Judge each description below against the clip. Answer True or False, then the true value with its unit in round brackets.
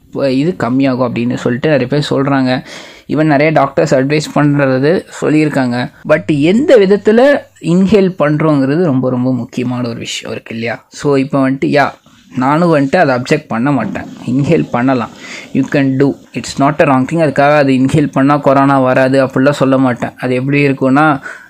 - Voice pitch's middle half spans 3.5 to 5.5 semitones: False (2.9 semitones)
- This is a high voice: False (140 Hz)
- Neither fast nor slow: False (160 wpm)